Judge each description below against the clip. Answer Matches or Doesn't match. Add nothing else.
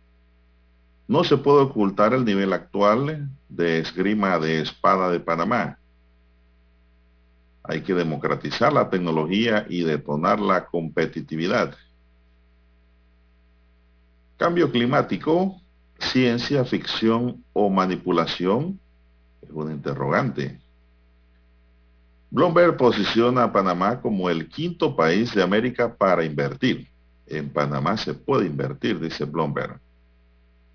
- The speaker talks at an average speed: Doesn't match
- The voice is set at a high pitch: Doesn't match